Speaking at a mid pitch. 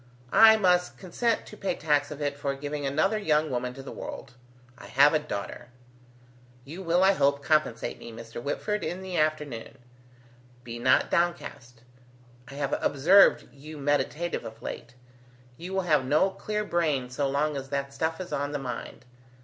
Yes: medium, 145 Hz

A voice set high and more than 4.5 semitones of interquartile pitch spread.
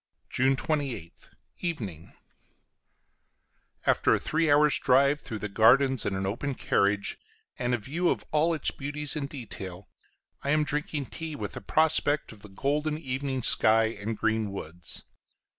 No: low, 135 Hz; wide, 5.5 semitones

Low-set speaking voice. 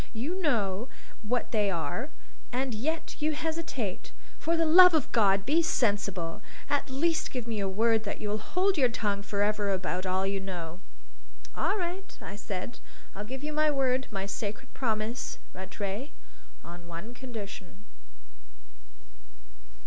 No: high, 220 Hz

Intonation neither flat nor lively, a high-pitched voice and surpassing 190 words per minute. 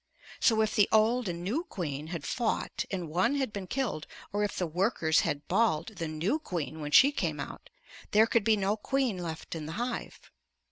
No: wide, 5.7 semitones; high, 200 Hz; average, 200 wpm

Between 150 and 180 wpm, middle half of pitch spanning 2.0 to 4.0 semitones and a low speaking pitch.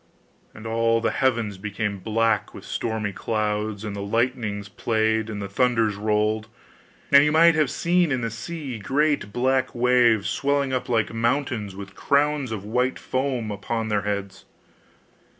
Yes: average, 155 wpm; average, 3.6 semitones; low, 115 Hz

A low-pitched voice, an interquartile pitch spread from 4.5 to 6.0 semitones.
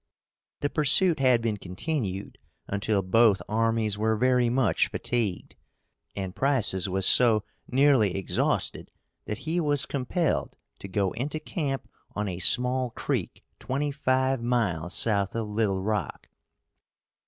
Yes: low, 115 Hz; average, 5.0 semitones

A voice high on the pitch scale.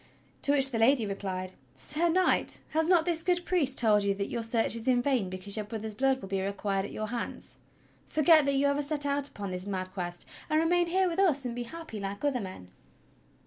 Yes: high, 245 Hz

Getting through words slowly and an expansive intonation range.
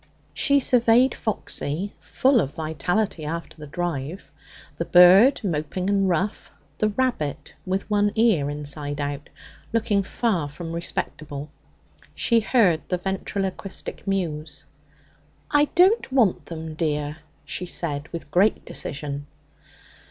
Yes: slow, 120 wpm; wide, 5.9 semitones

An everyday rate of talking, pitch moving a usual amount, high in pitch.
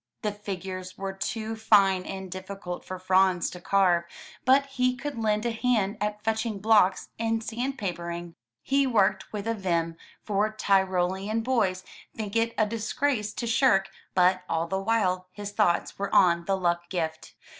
Yes: average, 160 wpm; average, 3.2 semitones; high, 200 Hz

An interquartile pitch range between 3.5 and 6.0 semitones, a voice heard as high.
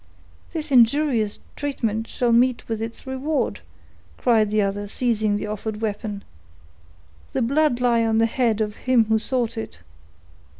No: average, 2.9 semitones; high, 230 Hz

